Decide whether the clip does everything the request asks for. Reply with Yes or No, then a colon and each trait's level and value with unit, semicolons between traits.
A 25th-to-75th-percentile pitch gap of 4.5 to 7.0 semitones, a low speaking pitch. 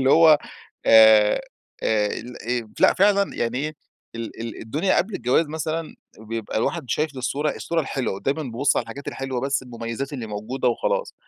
Yes: average, 4.8 semitones; low, 130 Hz